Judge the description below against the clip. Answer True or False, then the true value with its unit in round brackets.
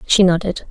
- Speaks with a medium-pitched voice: True (180 Hz)